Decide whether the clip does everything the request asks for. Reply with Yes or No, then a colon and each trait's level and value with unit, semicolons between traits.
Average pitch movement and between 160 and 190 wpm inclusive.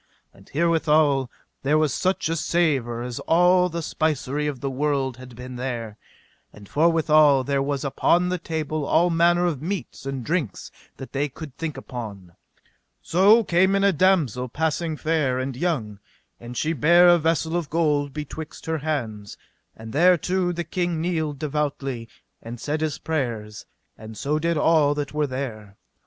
Yes: average, 4.3 semitones; average, 165 wpm